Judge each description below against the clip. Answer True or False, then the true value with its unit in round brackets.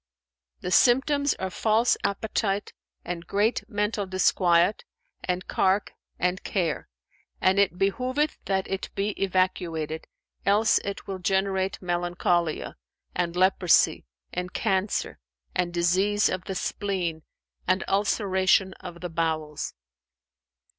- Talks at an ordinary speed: False (115 wpm)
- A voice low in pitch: False (190 Hz)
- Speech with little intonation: True (2.2 semitones)